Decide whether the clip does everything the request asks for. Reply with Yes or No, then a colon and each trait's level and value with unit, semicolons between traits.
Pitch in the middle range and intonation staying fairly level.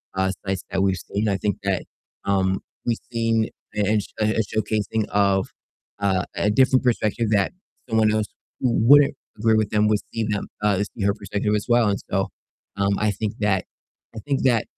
No: low, 105 Hz; narrow, 2.0 semitones